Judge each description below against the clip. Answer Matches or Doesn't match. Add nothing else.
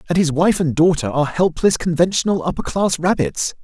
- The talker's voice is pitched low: Doesn't match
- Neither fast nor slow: Matches